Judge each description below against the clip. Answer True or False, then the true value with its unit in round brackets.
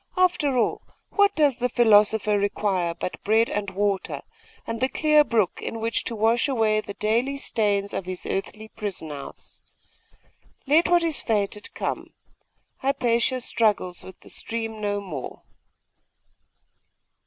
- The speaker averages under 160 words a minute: True (140 wpm)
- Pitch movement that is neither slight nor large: True (3.8 semitones)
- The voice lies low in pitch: False (220 Hz)